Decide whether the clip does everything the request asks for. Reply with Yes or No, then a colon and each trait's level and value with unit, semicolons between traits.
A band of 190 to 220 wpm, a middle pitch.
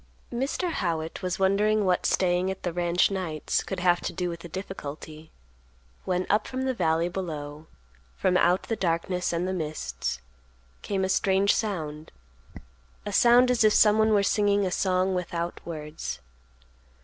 No: average, 160 wpm; medium, 180 Hz